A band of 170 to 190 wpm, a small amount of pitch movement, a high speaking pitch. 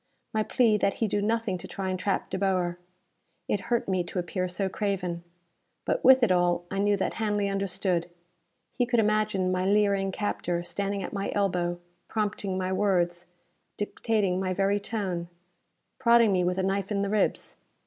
Yes: average, 180 wpm; narrow, 2.2 semitones; high, 195 Hz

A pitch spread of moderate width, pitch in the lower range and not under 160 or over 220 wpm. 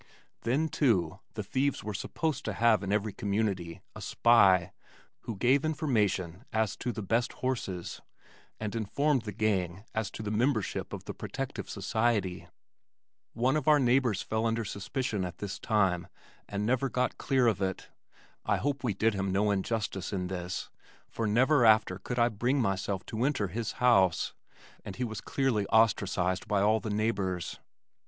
Yes: average, 3.9 semitones; low, 110 Hz; average, 165 wpm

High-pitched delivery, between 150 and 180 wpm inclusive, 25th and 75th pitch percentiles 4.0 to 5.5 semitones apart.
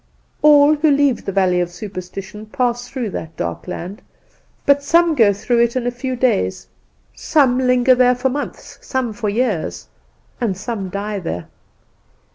Yes: high, 235 Hz; average, 160 wpm; average, 4.8 semitones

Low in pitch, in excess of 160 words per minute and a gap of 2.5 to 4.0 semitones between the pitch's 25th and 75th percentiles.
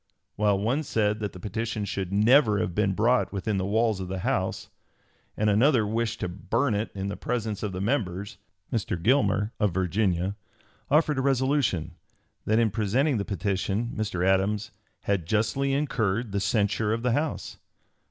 Yes: low, 105 Hz; average, 170 wpm; average, 3.1 semitones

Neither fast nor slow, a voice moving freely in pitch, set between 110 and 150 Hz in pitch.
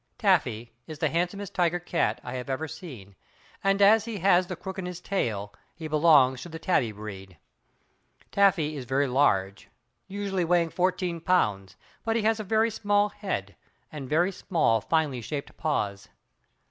No: average, 165 wpm; wide, 7.3 semitones; medium, 165 Hz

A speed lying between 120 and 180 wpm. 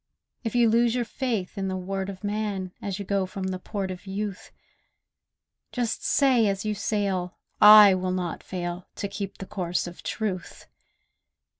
Yes: average, 175 wpm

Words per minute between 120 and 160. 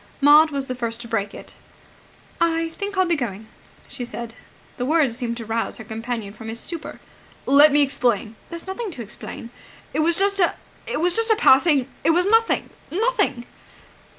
No: average, 185 wpm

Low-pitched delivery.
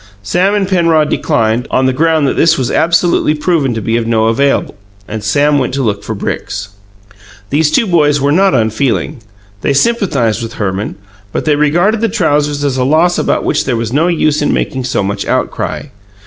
No: medium, 145 Hz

